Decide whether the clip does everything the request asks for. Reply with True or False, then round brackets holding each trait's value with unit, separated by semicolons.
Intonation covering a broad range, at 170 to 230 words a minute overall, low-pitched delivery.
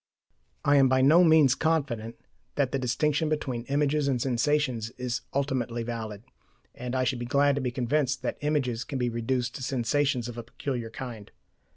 False (3.1 semitones; 180 wpm; 130 Hz)